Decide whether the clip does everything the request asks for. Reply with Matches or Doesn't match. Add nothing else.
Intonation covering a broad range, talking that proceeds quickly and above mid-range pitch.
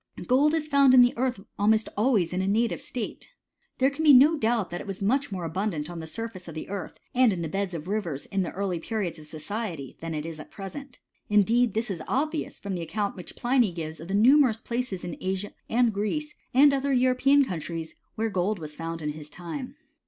Matches